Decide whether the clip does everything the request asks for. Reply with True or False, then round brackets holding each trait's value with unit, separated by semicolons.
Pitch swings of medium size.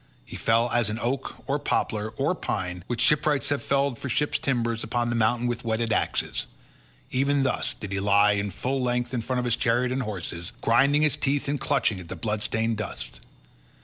True (4.0 semitones)